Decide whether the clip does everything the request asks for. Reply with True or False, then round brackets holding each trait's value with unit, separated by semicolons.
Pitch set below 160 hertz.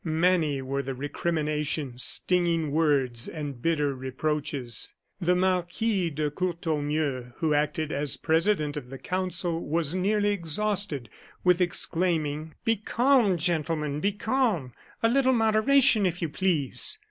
False (165 Hz)